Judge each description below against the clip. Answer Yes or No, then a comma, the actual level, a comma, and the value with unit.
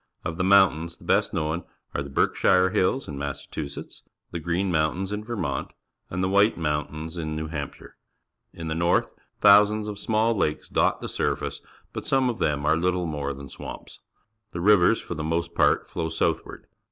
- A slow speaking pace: No, average, 175 wpm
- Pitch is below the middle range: Yes, very low, 85 Hz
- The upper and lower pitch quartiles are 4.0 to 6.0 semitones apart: Yes, average, 4.3 semitones